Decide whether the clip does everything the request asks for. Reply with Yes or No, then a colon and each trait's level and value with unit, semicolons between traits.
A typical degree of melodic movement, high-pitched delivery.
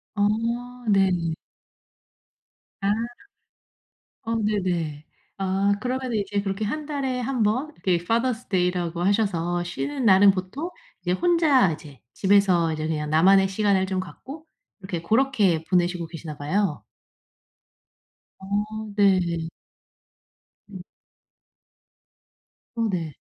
Yes: average, 4.4 semitones; high, 195 Hz